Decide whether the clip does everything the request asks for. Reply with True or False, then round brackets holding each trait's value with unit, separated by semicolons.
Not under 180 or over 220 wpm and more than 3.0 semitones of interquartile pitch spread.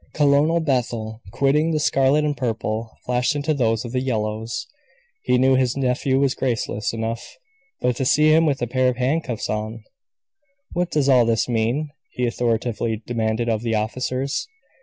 False (165 wpm; 3.4 semitones)